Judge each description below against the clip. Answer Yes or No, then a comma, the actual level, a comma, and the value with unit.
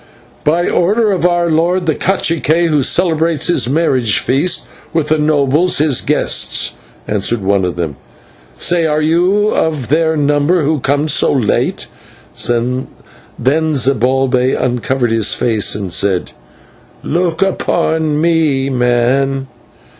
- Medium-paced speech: No, slow, 125 wpm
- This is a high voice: No, medium, 150 Hz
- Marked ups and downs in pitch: No, average, 4.8 semitones